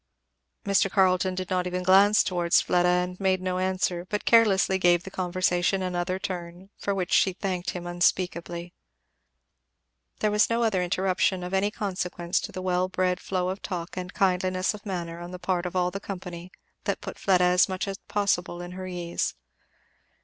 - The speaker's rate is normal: Yes, average, 180 wpm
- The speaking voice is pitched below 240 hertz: Yes, medium, 185 Hz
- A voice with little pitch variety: Yes, narrow, 1.3 semitones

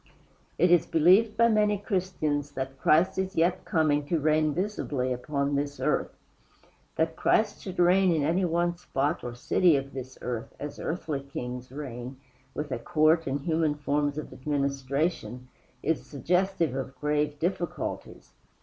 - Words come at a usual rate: Yes, average, 150 wpm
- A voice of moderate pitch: Yes, medium, 150 Hz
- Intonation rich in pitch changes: No, average, 4.1 semitones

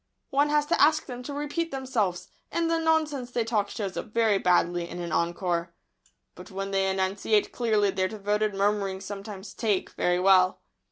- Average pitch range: Yes, average, 4.8 semitones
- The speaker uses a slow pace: No, average, 175 wpm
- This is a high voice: Yes, high, 205 Hz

